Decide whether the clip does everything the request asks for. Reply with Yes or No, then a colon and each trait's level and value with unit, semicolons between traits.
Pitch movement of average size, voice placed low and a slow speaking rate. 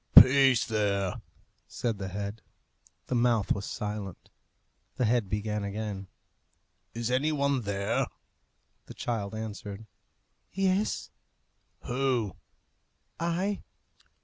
Yes: average, 4.3 semitones; low, 110 Hz; slow, 95 wpm